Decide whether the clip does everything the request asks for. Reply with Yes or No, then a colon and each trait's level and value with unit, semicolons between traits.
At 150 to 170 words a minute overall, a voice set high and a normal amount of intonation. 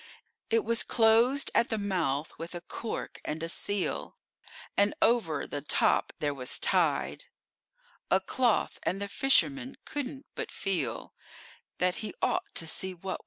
No: average, 160 wpm; high, 200 Hz; wide, 6.2 semitones